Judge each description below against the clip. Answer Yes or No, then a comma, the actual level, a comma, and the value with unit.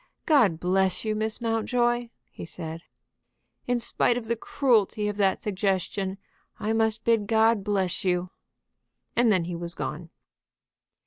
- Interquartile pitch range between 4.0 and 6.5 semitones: No, average, 3.5 semitones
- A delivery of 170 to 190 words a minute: No, average, 140 wpm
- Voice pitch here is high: Yes, high, 210 Hz